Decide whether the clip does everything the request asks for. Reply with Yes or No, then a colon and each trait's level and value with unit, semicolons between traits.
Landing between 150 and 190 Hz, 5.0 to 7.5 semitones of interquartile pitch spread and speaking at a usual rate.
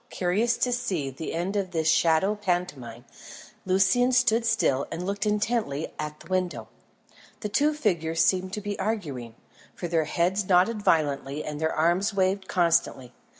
No: medium, 185 Hz; average, 4.6 semitones; average, 155 wpm